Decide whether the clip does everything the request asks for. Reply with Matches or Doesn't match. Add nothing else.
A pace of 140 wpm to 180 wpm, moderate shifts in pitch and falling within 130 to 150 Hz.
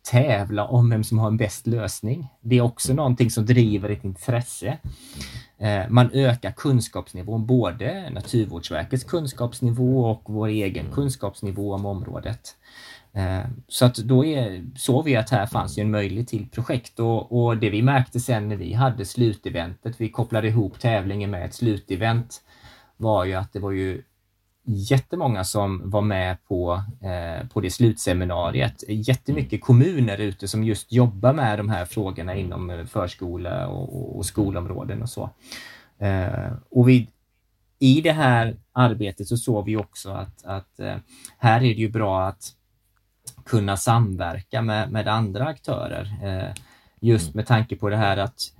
Doesn't match